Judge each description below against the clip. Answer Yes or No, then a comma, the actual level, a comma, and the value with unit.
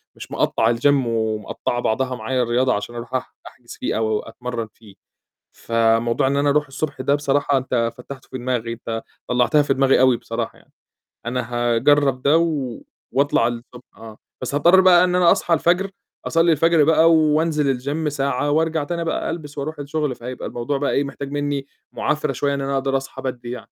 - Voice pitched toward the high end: No, low, 135 Hz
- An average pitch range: Yes, average, 3.6 semitones